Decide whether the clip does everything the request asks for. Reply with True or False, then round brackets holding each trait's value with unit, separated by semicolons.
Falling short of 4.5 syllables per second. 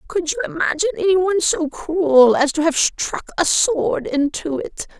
False (4.9 syllables/s)